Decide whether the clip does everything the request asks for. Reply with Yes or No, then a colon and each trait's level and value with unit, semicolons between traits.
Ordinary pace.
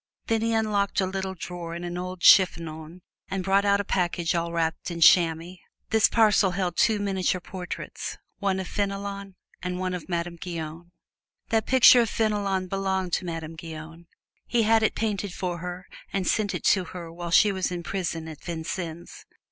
Yes: average, 180 wpm